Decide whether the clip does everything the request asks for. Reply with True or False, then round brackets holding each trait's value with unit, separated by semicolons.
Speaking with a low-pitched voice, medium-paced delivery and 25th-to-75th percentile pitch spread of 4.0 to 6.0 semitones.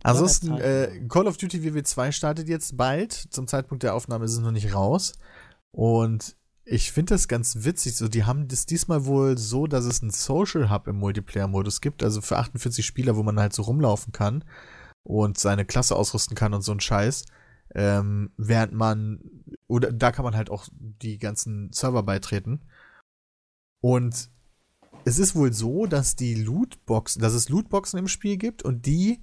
True (120 Hz; 180 wpm; 4.6 semitones)